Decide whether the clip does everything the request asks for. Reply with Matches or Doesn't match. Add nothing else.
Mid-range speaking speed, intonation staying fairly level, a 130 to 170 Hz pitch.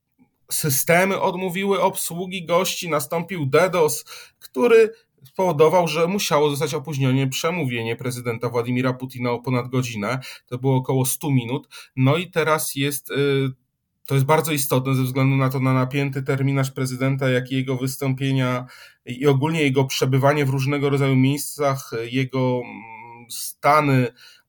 Doesn't match